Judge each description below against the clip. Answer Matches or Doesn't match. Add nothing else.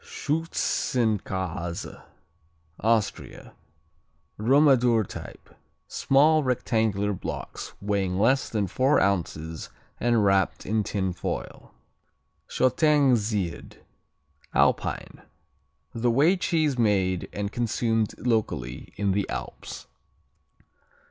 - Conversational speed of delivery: Doesn't match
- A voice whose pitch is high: Doesn't match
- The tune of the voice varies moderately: Matches